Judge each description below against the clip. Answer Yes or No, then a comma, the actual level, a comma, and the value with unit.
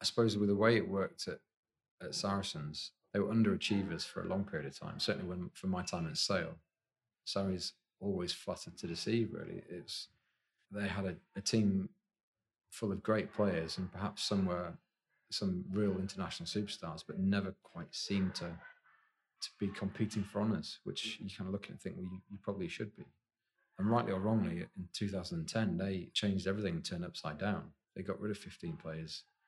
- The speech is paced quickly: No, average, 195 wpm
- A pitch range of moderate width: No, narrow, 2.2 semitones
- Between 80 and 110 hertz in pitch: Yes, low, 100 Hz